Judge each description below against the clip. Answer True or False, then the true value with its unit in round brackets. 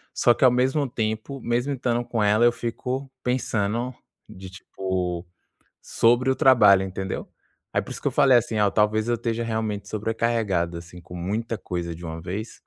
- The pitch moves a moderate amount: True (4.0 semitones)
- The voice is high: False (110 Hz)